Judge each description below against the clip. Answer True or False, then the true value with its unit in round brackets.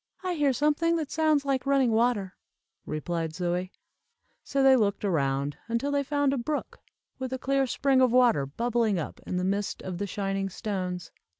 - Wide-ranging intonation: True (6.8 semitones)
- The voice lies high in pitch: True (235 Hz)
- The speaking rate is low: False (180 wpm)